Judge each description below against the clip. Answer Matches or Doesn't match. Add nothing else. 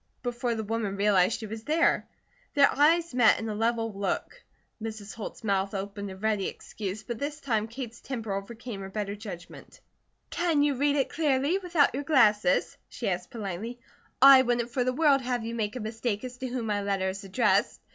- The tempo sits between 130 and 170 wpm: Doesn't match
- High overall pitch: Matches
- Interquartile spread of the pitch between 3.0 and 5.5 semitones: Matches